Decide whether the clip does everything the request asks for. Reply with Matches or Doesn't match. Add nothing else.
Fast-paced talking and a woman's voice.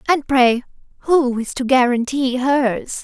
Doesn't match